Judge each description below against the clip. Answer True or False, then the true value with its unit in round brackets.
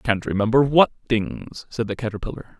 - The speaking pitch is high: False (115 Hz)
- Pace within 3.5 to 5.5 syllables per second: True (5.2 syllables/s)